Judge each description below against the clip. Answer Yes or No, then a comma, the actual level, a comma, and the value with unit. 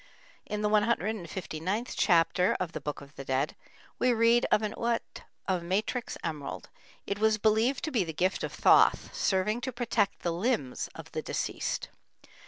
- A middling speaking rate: Yes, average, 170 wpm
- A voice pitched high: Yes, high, 205 Hz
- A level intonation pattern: No, average, 5.0 semitones